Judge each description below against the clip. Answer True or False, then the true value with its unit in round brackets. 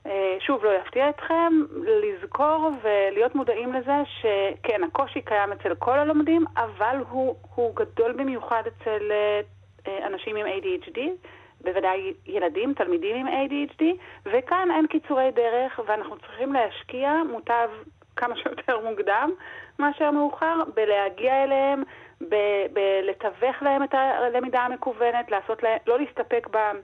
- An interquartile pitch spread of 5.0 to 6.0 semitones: True (5.6 semitones)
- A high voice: True (255 Hz)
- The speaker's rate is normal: True (120 wpm)